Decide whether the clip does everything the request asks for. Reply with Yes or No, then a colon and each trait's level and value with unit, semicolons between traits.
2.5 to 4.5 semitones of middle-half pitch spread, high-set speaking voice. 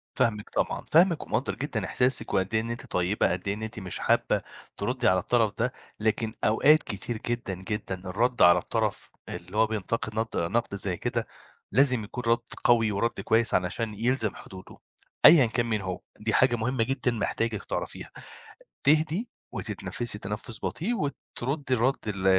No: average, 3.4 semitones; low, 115 Hz